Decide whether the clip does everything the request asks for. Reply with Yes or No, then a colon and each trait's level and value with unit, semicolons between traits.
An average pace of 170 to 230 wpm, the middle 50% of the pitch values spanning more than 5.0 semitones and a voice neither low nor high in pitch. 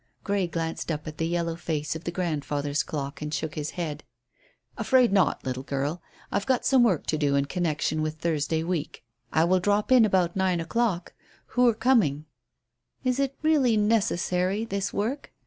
Yes: average, 175 wpm; wide, 5.5 semitones; medium, 170 Hz